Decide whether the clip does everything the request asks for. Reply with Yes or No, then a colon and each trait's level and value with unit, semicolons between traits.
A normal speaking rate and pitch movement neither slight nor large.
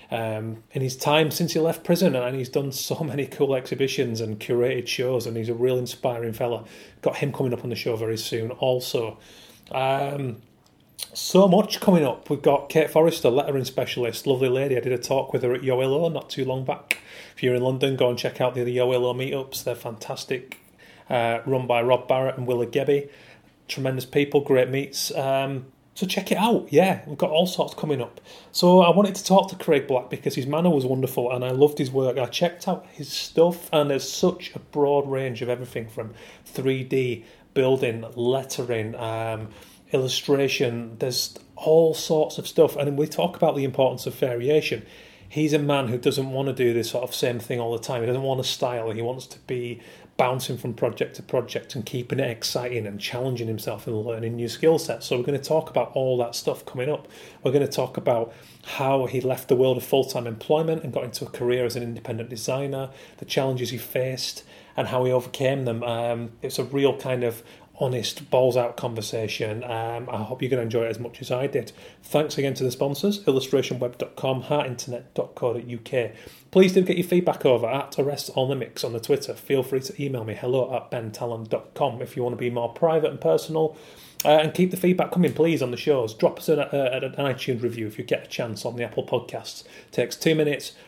No: fast, 210 wpm; average, 3.2 semitones